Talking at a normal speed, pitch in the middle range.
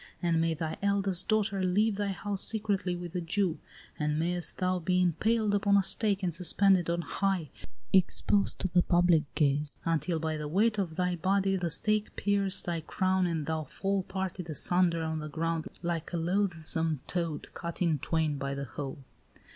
Yes: average, 180 wpm; medium, 175 Hz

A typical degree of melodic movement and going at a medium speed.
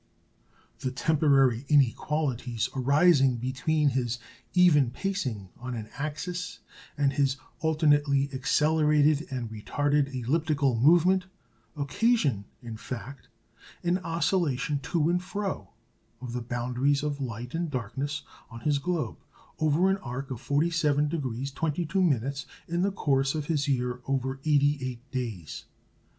No: average, 3.7 semitones; slow, 120 wpm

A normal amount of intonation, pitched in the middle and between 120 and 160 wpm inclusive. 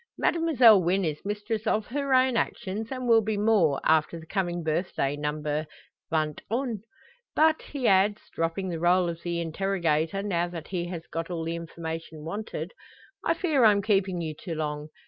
No: average, 4.8 semitones; medium, 180 Hz; average, 175 wpm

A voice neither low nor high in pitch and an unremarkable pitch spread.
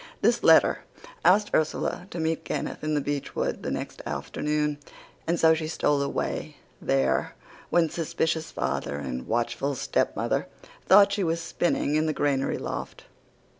Yes: medium, 155 Hz; average, 3.0 semitones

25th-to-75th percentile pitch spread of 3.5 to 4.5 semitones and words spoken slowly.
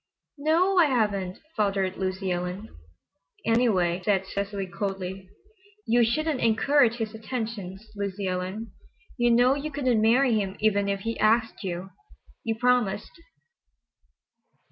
Yes: average, 3.9 semitones; slow, 120 wpm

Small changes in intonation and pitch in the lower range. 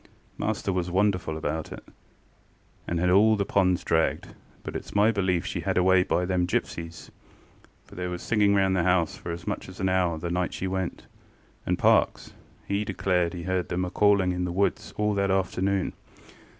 Yes: narrow, 1.9 semitones; very low, 90 Hz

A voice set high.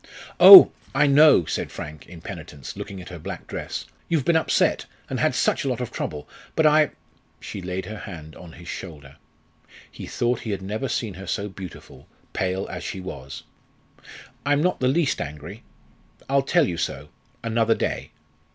No: low, 100 Hz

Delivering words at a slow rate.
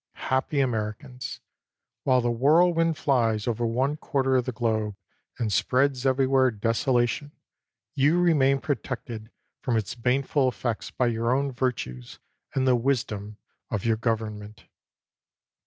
Yes: slow, 130 wpm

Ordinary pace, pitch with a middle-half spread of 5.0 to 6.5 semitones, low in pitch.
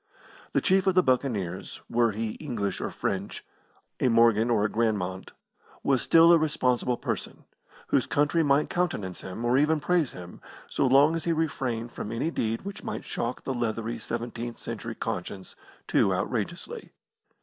Yes: average, 160 wpm; average, 5.3 semitones; low, 120 Hz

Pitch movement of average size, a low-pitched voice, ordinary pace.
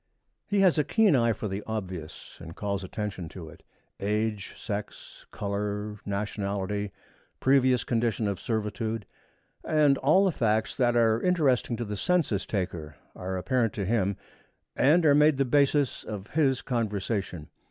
Yes: average, 4.8 semitones; low, 110 Hz; average, 150 wpm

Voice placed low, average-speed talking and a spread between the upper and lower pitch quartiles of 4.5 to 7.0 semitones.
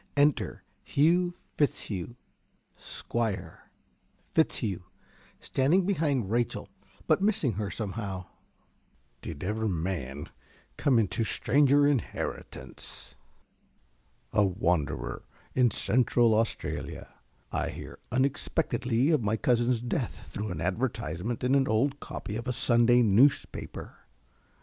No: low, 115 Hz; slow, 105 wpm; wide, 5.5 semitones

